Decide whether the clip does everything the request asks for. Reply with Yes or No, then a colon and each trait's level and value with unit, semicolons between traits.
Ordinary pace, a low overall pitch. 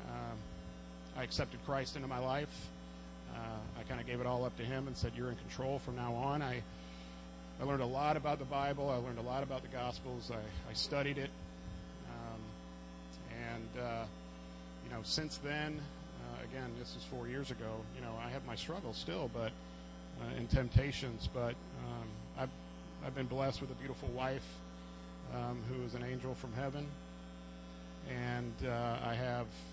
Yes: average, 180 wpm; low, 115 Hz